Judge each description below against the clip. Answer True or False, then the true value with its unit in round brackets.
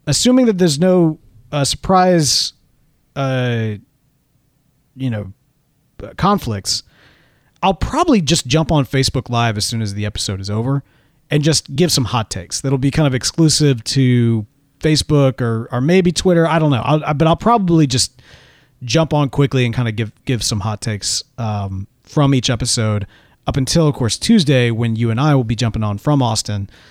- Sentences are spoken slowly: False (180 wpm)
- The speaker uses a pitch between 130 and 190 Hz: True (135 Hz)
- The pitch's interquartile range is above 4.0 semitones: True (4.9 semitones)